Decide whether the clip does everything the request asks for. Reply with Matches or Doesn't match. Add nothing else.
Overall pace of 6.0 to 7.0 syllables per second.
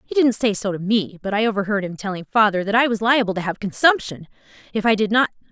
Matches